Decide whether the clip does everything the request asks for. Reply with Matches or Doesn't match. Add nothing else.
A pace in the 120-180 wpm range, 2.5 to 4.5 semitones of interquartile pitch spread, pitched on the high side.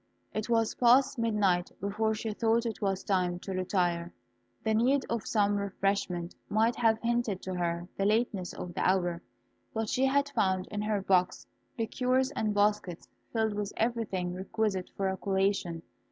Matches